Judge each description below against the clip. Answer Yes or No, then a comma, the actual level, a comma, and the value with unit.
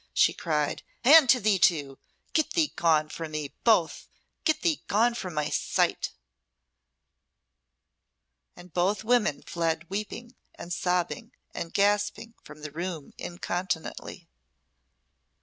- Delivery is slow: Yes, slow, 120 wpm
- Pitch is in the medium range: Yes, medium, 180 Hz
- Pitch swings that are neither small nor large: No, wide, 5.9 semitones